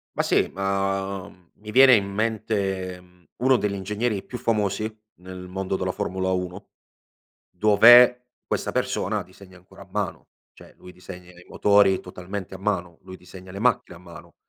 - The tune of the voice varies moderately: No, narrow, 2.3 semitones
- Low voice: Yes, very low, 95 Hz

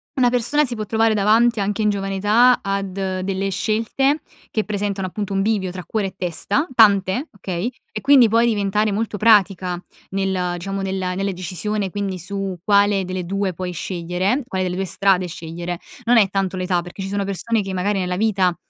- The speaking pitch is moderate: No, high, 195 Hz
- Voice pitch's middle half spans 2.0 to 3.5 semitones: Yes, narrow, 2.4 semitones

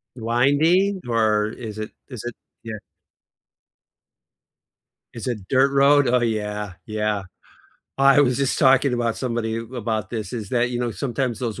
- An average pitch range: Yes, average, 3.4 semitones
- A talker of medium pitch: No, low, 120 Hz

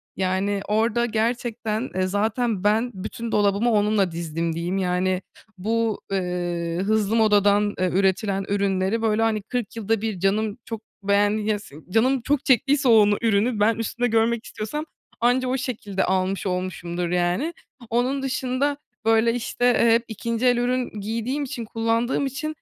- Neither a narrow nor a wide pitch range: Yes, average, 3.4 semitones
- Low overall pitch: No, high, 220 Hz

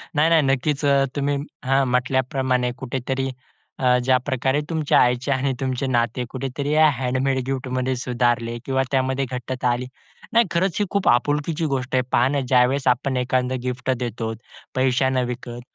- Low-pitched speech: Yes, low, 130 Hz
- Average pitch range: No, narrow, 1.7 semitones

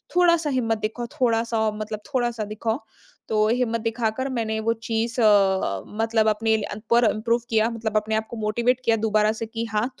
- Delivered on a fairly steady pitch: Yes, narrow, 1.6 semitones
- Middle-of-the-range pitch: No, high, 225 Hz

